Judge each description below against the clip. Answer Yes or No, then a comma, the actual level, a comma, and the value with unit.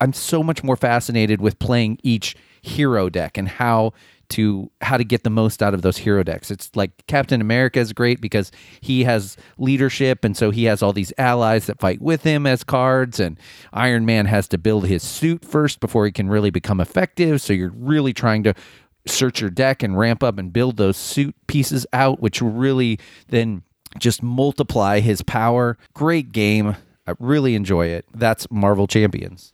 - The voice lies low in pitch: Yes, low, 115 Hz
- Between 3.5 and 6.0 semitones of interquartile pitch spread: Yes, average, 4.2 semitones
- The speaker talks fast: No, average, 190 wpm